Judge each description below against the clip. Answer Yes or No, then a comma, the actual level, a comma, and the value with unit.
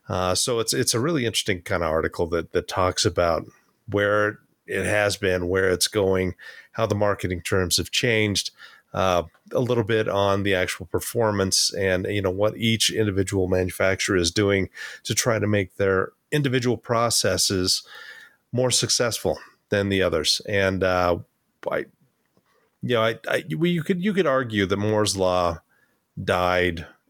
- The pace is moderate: Yes, average, 160 wpm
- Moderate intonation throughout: Yes, average, 3.1 semitones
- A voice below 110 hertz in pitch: Yes, low, 100 Hz